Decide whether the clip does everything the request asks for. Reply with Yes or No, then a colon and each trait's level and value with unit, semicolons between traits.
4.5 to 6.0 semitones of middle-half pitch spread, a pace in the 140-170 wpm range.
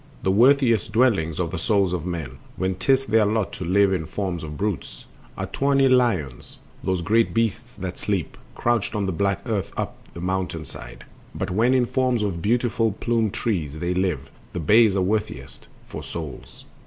No: average, 4.8 semitones; average, 180 wpm